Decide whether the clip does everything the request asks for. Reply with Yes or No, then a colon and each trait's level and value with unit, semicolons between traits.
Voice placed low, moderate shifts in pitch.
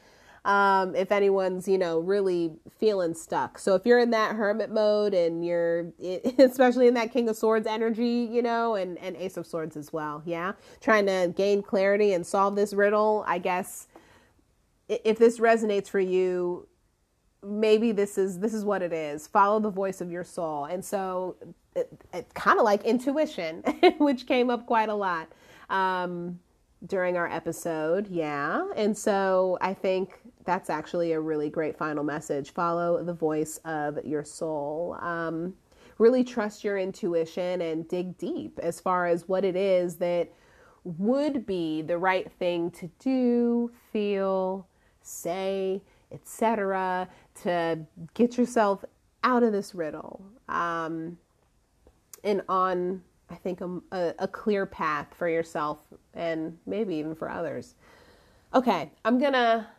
No: medium, 185 Hz; average, 3.8 semitones